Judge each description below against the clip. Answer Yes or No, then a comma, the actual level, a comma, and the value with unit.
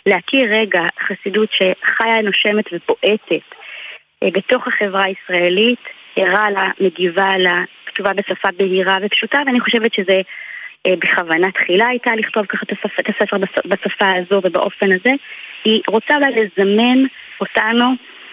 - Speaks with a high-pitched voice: Yes, high, 200 Hz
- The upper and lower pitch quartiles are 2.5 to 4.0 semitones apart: Yes, average, 2.9 semitones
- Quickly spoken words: No, average, 130 wpm